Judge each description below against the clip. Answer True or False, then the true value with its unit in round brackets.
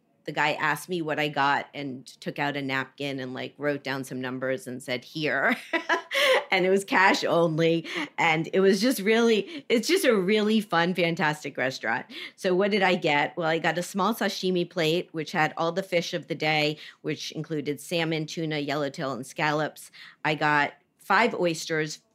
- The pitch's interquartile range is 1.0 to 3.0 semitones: False (4.3 semitones)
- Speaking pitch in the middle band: True (160 Hz)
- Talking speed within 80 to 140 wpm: False (185 wpm)